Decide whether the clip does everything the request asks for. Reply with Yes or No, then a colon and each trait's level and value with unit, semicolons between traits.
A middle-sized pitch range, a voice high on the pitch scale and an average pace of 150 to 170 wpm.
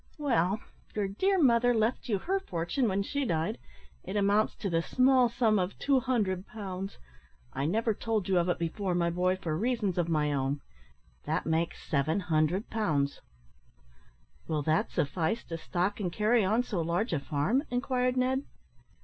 No: wide, 5.9 semitones; high, 195 Hz; average, 165 wpm